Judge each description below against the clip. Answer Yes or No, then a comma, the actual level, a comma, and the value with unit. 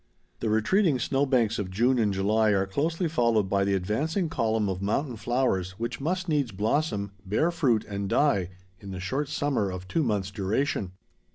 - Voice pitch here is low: Yes, low, 110 Hz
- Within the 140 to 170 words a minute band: No, average, 180 wpm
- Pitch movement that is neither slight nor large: No, wide, 6.3 semitones